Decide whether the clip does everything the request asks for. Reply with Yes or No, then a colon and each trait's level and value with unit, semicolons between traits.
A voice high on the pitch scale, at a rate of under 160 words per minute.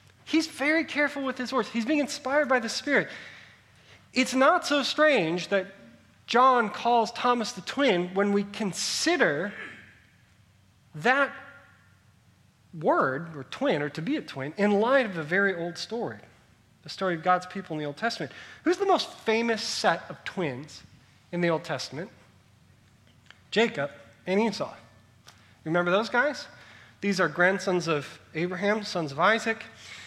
Yes: high, 195 Hz; average, 150 wpm